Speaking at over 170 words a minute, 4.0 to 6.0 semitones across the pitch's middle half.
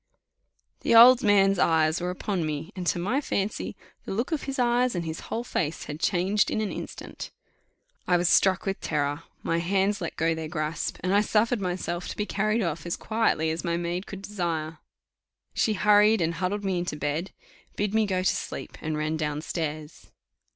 Yes: average, 195 wpm; average, 4.3 semitones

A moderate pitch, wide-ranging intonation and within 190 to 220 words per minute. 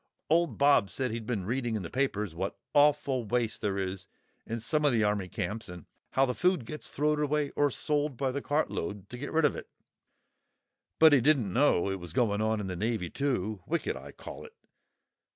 No: low, 120 Hz; wide, 5.9 semitones; fast, 205 wpm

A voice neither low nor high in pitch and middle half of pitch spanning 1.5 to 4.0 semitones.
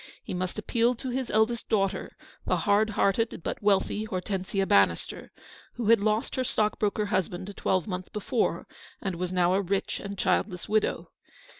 No: high, 200 Hz; average, 2.8 semitones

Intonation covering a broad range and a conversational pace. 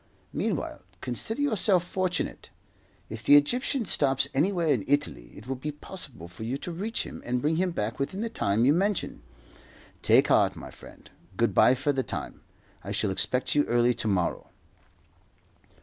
Yes: wide, 7.1 semitones; average, 170 wpm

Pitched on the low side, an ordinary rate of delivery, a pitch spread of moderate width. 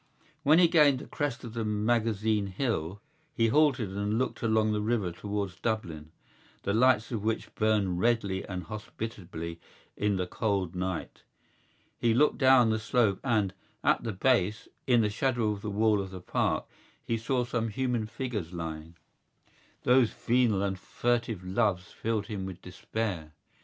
Yes: low, 110 Hz; average, 160 wpm; average, 3.7 semitones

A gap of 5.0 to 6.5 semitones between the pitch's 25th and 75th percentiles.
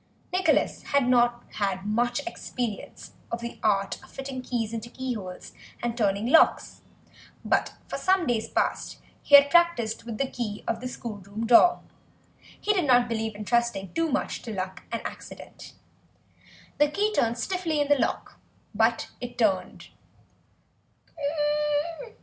No: average, 4.1 semitones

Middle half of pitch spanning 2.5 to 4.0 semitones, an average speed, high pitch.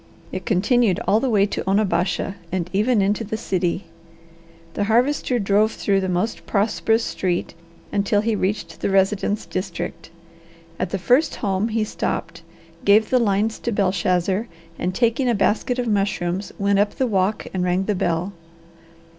Yes: average, 2.8 semitones; average, 160 wpm; high, 200 Hz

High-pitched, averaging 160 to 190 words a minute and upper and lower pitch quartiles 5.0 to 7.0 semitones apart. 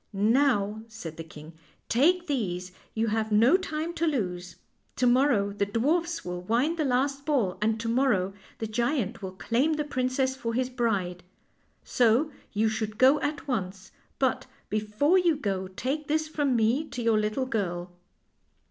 Yes: high, 235 Hz; average, 170 wpm; wide, 5.5 semitones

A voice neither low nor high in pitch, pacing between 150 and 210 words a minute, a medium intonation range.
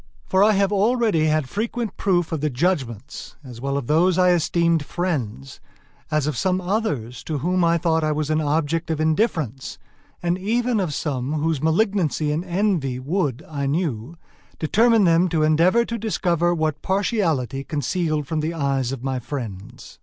Yes: medium, 160 Hz; average, 170 wpm; average, 4.6 semitones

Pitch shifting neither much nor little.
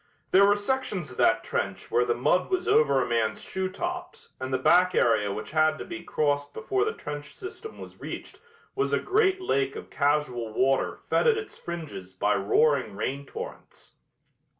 No: wide, 8.8 semitones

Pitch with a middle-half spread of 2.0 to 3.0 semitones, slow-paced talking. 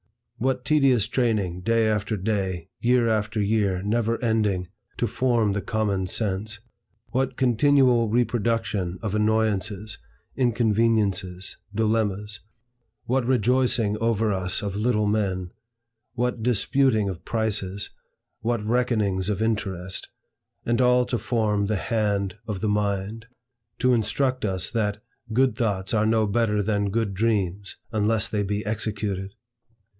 Yes: narrow, 2.6 semitones; slow, 125 wpm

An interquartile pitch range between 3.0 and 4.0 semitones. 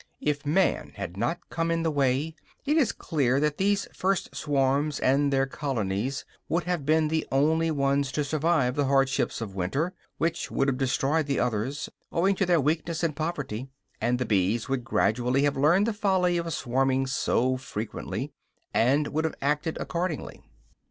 Yes: average, 3.7 semitones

